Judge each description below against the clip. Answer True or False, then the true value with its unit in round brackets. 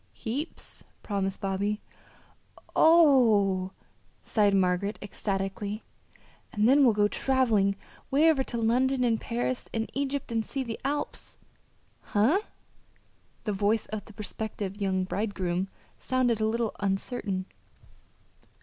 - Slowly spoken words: True (120 wpm)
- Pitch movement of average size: True (4.1 semitones)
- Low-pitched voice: False (215 Hz)